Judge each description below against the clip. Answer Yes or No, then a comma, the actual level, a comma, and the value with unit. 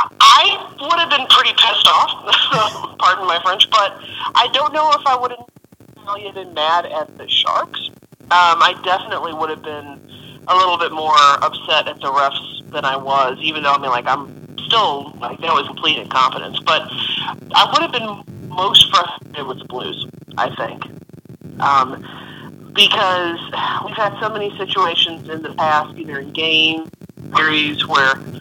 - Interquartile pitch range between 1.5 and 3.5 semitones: No, wide, 5.4 semitones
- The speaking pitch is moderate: Yes, medium, 160 Hz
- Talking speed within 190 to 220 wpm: No, average, 170 wpm